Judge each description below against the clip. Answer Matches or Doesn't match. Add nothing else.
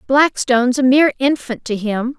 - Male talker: Doesn't match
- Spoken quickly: Doesn't match